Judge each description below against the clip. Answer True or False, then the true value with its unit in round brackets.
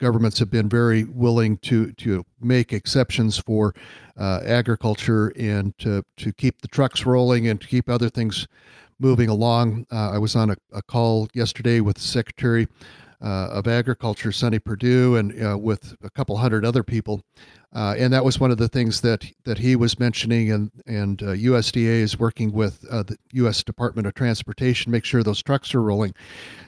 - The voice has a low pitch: True (115 Hz)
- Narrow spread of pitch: True (2.2 semitones)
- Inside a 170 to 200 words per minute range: True (185 wpm)